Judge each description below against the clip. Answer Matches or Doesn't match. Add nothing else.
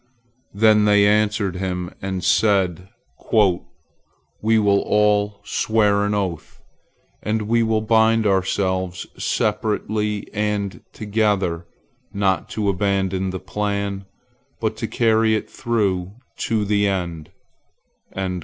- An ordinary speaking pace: Doesn't match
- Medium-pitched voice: Doesn't match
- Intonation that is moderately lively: Doesn't match